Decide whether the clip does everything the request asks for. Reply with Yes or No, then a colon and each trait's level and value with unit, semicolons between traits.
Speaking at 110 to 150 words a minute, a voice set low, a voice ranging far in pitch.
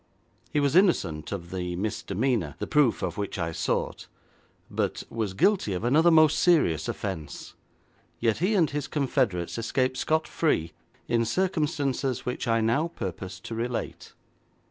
Yes: average, 145 wpm; low, 115 Hz; wide, 8.0 semitones